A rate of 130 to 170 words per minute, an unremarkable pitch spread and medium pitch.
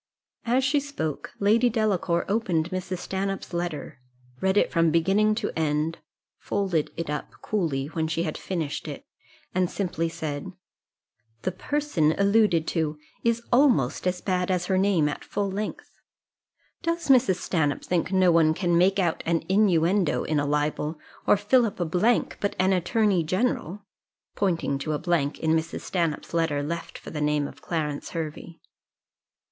Yes: average, 160 wpm; average, 4.1 semitones; medium, 175 Hz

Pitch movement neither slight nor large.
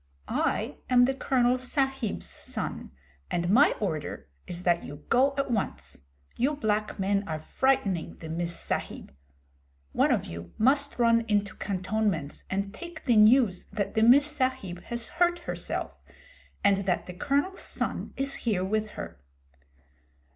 No: wide, 6.3 semitones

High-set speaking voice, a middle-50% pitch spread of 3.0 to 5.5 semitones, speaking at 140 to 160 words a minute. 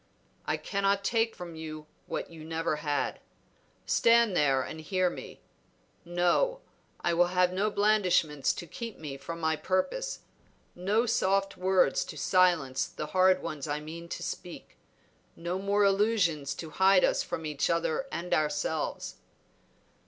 No: medium, 180 Hz; average, 3.9 semitones; average, 145 wpm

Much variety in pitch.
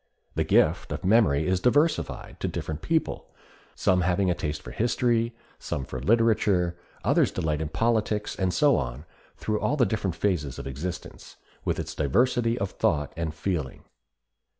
Yes: wide, 7.0 semitones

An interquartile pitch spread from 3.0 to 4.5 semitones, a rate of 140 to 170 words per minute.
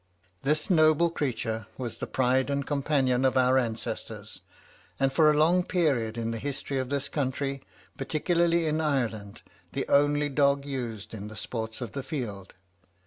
Yes: average, 3.8 semitones; average, 160 wpm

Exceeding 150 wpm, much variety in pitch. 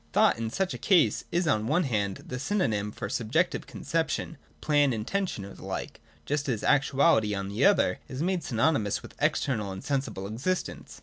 Yes: average, 185 wpm; wide, 7.1 semitones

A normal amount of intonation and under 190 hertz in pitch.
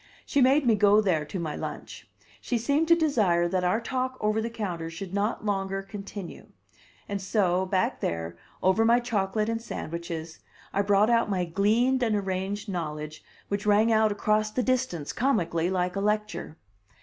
No: average, 3.8 semitones; high, 205 Hz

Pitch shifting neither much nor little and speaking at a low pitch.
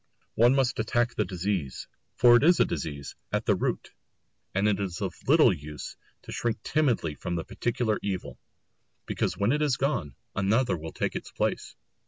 No: wide, 5.7 semitones; low, 105 Hz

